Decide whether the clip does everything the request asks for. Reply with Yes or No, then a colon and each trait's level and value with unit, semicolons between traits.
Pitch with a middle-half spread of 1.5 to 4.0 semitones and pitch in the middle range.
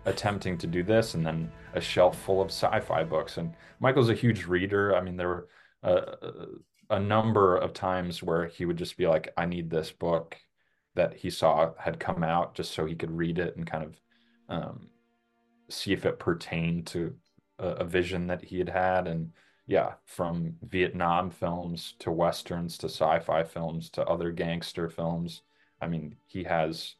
No: narrow, 2.5 semitones; very low, 85 Hz